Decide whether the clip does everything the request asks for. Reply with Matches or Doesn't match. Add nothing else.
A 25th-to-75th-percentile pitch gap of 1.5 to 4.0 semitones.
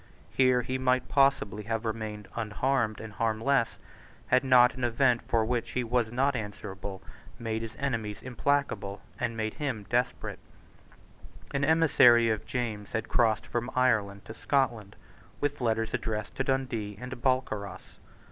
Matches